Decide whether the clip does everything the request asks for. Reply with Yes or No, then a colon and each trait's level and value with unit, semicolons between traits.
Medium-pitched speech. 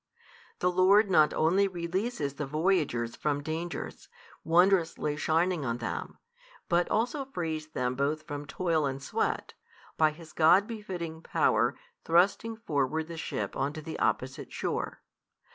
Yes: medium, 165 Hz